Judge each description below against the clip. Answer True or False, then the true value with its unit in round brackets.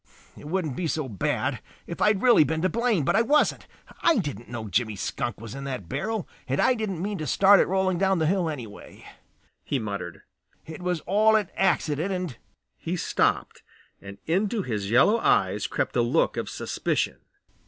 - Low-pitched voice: False (170 Hz)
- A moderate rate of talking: True (195 wpm)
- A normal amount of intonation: False (7.8 semitones)